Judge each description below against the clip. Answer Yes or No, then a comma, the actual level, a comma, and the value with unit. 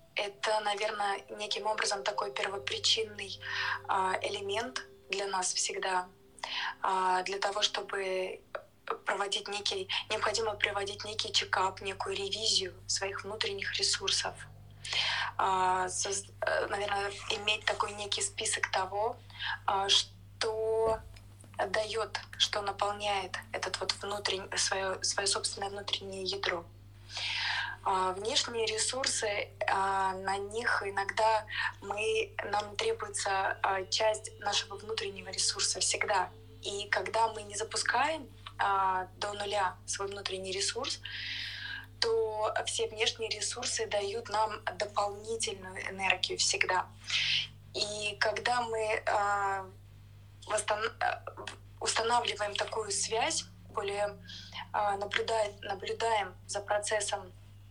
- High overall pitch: Yes, high, 205 Hz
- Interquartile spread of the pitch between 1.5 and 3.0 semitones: Yes, narrow, 2.4 semitones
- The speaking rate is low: Yes, slow, 90 wpm